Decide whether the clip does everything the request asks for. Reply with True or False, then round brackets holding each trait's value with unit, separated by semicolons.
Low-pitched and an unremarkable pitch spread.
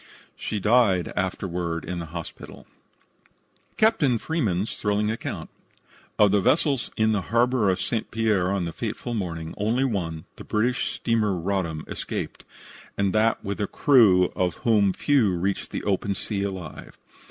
True (100 Hz; 3.9 semitones)